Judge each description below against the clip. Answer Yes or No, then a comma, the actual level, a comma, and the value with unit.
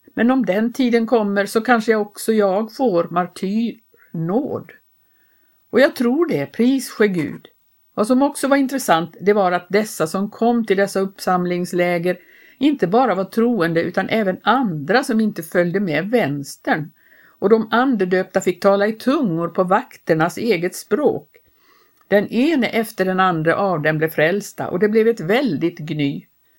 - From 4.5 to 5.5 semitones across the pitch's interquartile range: Yes, average, 4.9 semitones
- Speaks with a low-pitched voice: No, high, 205 Hz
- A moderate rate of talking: Yes, average, 160 wpm